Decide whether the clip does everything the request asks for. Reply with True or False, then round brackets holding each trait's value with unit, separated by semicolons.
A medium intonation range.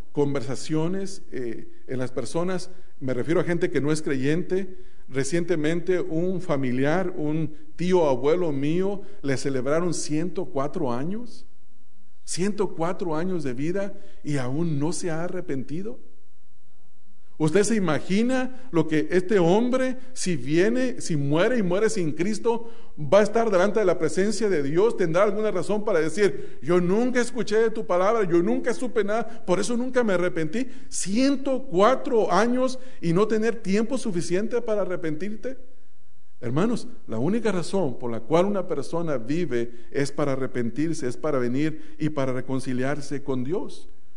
False (5.9 semitones)